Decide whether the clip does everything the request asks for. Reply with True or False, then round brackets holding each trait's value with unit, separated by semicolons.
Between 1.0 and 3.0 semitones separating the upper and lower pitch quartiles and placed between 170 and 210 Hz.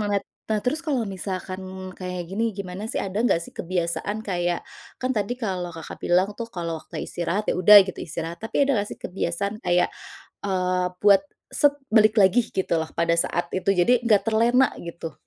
False (3.7 semitones; 190 Hz)